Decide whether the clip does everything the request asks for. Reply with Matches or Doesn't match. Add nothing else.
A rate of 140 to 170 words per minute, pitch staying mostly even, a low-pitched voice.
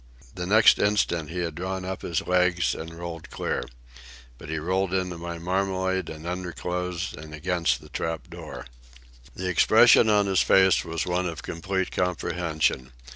Matches